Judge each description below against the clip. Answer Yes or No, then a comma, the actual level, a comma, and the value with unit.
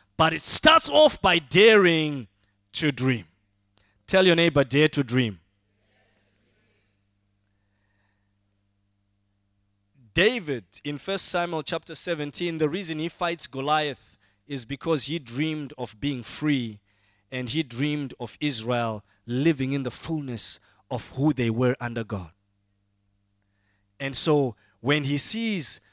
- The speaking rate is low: Yes, slow, 120 wpm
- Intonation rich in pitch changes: Yes, wide, 7.3 semitones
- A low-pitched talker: Yes, low, 125 Hz